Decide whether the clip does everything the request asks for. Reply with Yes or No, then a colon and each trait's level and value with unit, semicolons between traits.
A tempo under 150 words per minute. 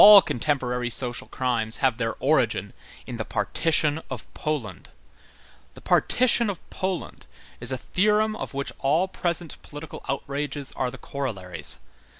Yes: average, 140 wpm